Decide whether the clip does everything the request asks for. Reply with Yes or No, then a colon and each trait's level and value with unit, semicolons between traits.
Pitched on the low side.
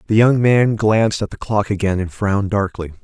Yes: low, 105 Hz